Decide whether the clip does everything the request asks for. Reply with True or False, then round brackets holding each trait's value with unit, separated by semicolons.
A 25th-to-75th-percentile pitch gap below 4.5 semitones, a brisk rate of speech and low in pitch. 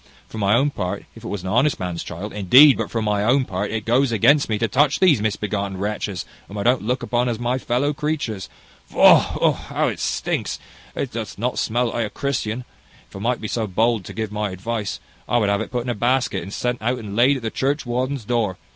True (3.5 semitones; 235 wpm; 115 Hz)